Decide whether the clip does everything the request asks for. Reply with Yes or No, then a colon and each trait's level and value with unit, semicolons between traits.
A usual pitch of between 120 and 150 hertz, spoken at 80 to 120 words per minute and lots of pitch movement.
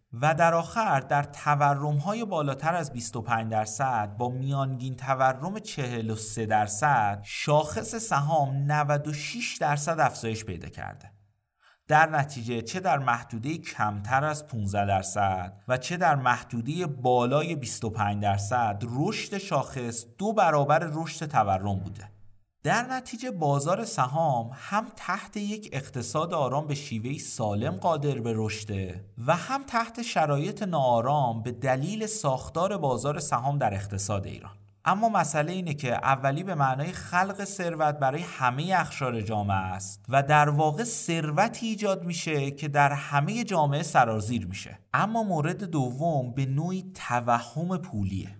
No: medium, 140 Hz; average, 130 wpm; wide, 6.0 semitones